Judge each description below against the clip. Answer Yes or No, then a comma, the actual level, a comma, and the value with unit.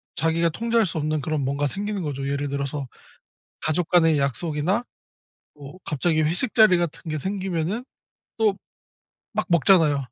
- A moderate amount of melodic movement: Yes, average, 4.5 semitones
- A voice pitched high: No, medium, 160 Hz